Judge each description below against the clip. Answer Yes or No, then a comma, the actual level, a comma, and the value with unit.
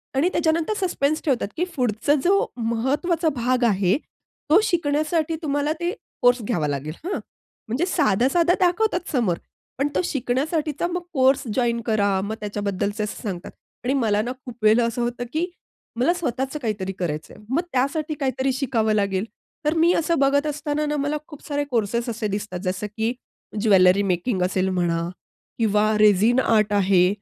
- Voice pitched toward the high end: Yes, high, 245 Hz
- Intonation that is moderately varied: No, wide, 6.4 semitones